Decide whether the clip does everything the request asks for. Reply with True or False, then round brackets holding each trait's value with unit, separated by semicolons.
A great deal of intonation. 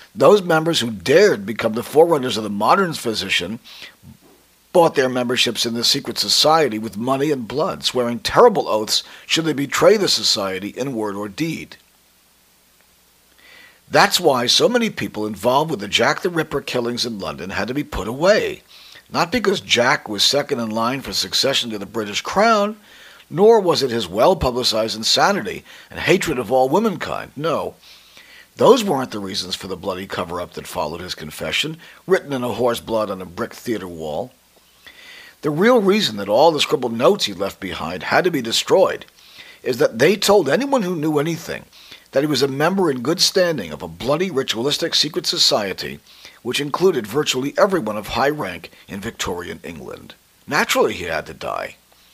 True (8.6 semitones)